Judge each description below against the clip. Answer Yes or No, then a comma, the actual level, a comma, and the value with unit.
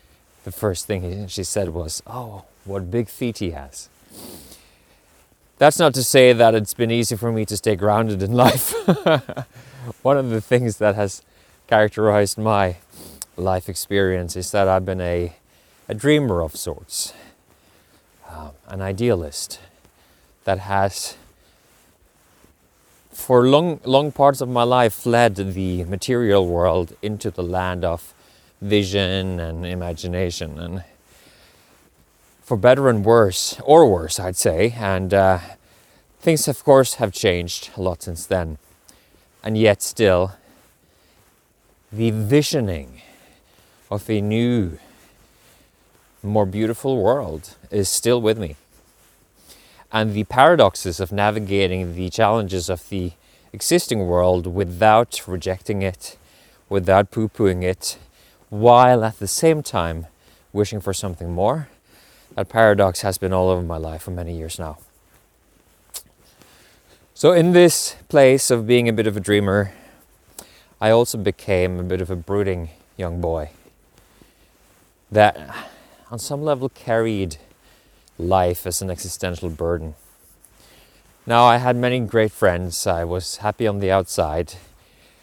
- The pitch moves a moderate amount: Yes, average, 4.1 semitones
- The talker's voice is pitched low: Yes, low, 100 Hz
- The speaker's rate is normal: No, slow, 130 wpm